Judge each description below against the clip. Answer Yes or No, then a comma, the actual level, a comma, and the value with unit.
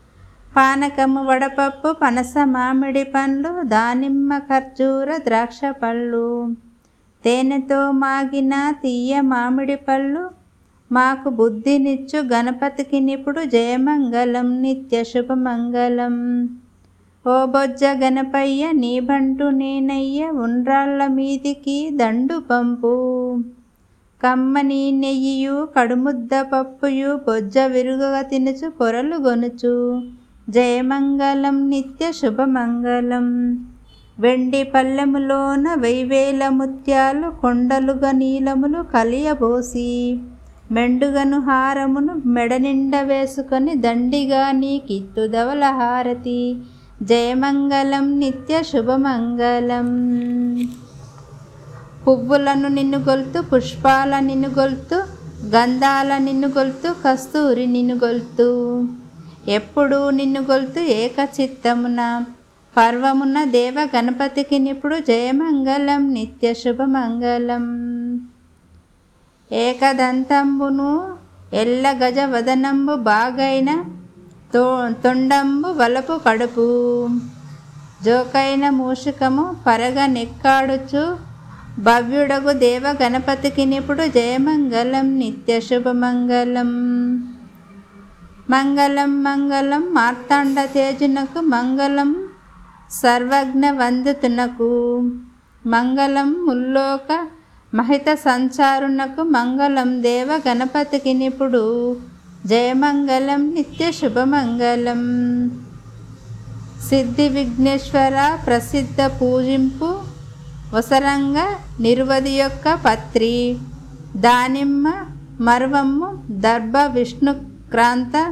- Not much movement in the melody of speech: Yes, narrow, 2.3 semitones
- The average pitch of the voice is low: No, very high, 265 Hz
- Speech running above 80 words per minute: No, slow, 70 wpm